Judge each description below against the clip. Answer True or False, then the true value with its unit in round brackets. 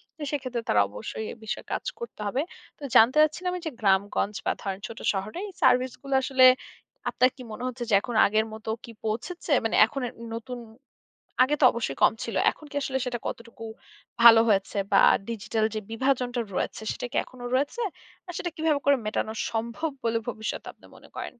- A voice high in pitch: True (240 Hz)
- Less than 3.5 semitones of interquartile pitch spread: False (3.8 semitones)